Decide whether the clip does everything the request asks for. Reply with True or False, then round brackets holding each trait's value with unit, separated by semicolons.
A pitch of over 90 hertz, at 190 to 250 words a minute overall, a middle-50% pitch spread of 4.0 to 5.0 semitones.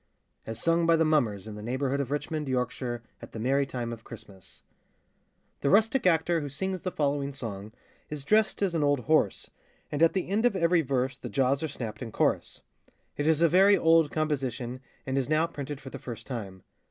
True (140 Hz; 205 wpm; 4.7 semitones)